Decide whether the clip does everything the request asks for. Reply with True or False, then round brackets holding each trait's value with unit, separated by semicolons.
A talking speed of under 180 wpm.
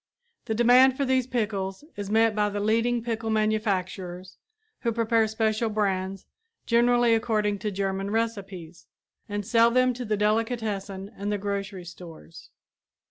True (140 wpm)